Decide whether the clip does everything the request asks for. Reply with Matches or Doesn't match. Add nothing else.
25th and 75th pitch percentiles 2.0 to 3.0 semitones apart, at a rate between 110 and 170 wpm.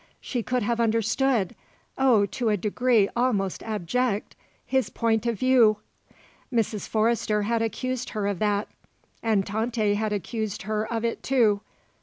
Matches